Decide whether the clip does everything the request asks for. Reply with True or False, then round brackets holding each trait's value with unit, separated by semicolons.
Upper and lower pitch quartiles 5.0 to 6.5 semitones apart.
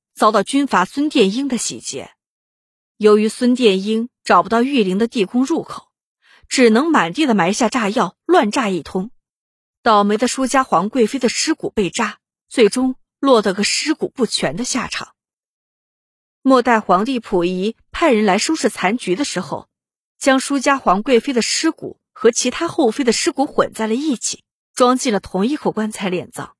False (4.5 semitones)